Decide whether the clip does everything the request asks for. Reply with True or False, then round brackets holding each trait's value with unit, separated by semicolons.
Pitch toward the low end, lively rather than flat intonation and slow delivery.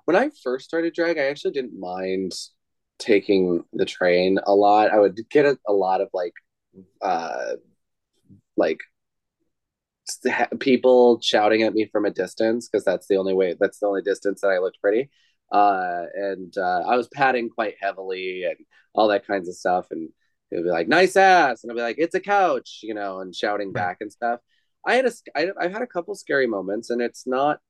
False (110 Hz; 7.1 semitones; 200 wpm)